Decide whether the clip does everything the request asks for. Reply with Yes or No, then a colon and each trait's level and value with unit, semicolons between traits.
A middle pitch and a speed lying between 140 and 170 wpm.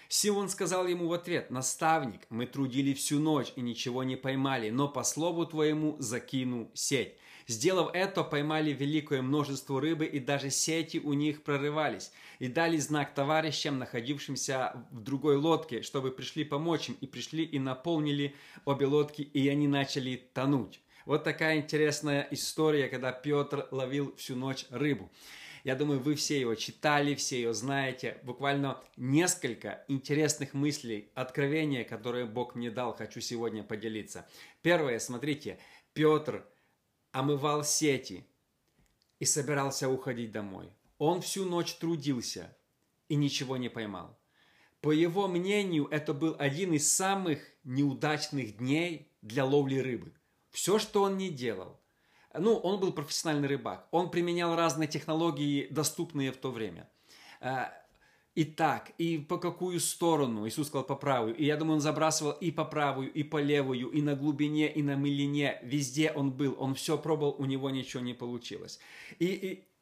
Yes: medium, 145 Hz; average, 150 wpm